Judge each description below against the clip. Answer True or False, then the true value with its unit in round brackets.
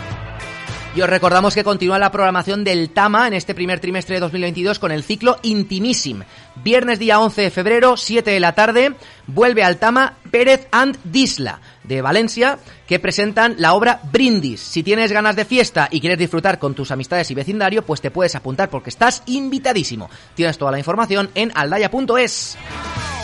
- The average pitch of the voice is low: False (195 Hz)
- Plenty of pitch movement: True (5.7 semitones)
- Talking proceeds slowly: False (175 wpm)